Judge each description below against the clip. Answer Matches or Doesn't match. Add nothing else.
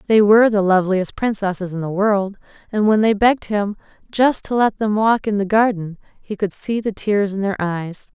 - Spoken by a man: Doesn't match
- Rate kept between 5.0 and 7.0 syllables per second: Matches